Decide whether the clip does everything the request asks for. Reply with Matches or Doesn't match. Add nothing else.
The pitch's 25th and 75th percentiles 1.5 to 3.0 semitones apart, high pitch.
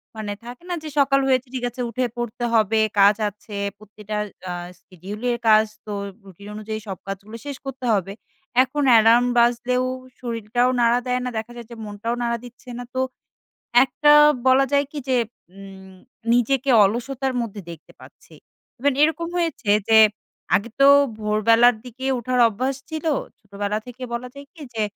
Doesn't match